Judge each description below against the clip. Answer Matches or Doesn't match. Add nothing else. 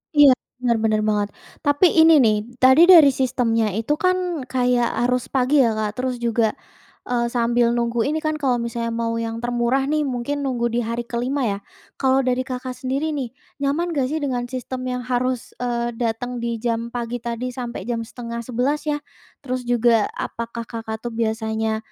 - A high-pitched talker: Matches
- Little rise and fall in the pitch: Matches